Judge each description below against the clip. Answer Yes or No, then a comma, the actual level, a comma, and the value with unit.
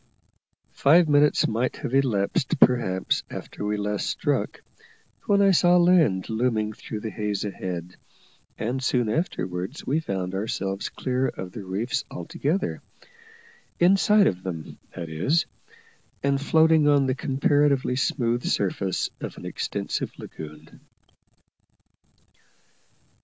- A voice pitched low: Yes, low, 120 Hz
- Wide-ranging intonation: Yes, wide, 7.1 semitones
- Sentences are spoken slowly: Yes, slow, 120 wpm